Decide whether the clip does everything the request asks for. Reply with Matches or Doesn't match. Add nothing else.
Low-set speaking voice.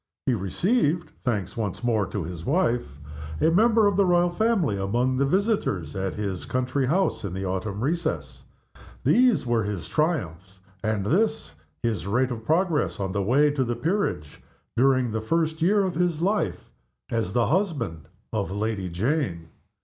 Matches